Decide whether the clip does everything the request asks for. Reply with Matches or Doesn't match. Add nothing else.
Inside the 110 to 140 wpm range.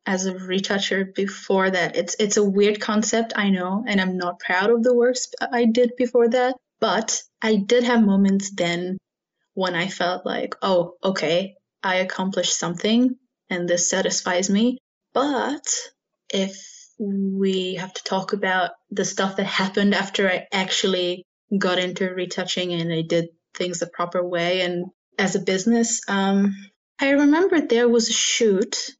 Doesn't match